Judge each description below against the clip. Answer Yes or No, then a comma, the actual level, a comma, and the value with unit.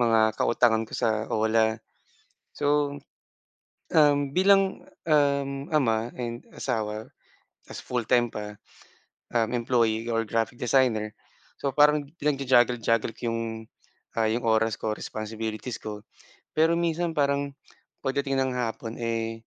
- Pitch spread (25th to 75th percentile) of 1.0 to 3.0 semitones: No, average, 4.0 semitones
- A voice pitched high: No, low, 120 Hz